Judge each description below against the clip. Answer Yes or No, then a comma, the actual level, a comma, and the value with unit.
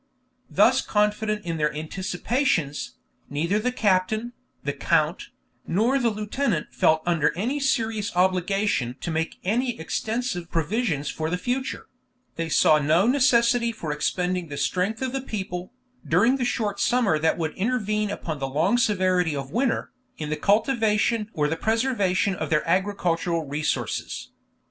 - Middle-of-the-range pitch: No, high, 195 Hz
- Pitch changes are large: Yes, wide, 6.0 semitones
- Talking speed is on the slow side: No, average, 145 wpm